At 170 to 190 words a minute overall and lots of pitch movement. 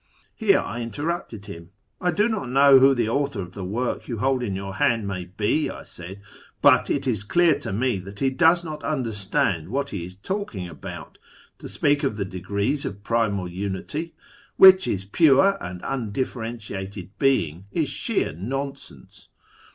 Yes: average, 175 wpm; wide, 6.3 semitones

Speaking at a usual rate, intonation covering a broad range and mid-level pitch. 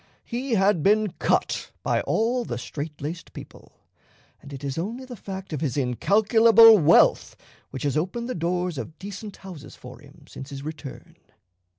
Yes: average, 170 wpm; wide, 7.0 semitones; medium, 175 Hz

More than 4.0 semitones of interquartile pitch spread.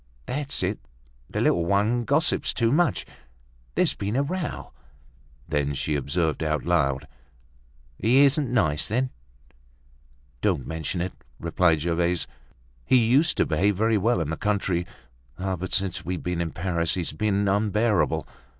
Yes: wide, 5.5 semitones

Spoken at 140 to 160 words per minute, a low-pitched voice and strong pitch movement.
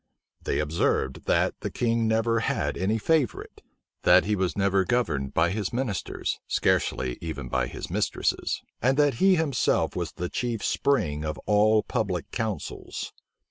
Yes: average, 150 wpm; low, 105 Hz; wide, 6.4 semitones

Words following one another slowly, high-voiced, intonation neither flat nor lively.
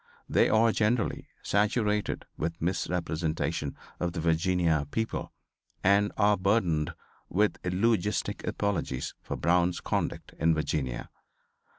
No: slow, 105 wpm; very low, 90 Hz; average, 4.2 semitones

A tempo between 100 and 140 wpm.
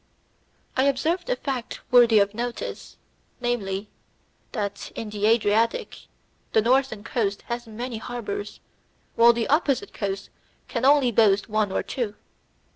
Yes: slow, 135 wpm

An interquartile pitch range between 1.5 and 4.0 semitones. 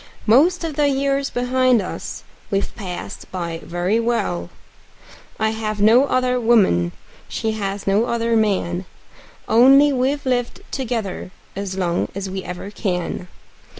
No: average, 4.9 semitones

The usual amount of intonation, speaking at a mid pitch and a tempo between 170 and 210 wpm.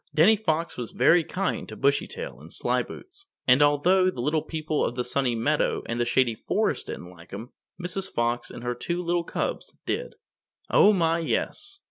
No: wide, 6.8 semitones; medium, 155 Hz; average, 180 wpm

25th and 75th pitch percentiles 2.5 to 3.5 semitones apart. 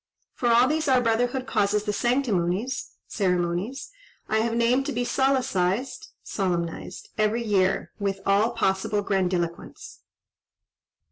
No: average, 4.4 semitones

